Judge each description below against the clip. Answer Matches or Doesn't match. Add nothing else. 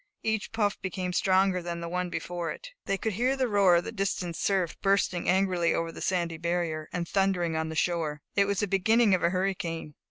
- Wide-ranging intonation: Doesn't match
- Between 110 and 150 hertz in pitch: Doesn't match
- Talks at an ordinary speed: Doesn't match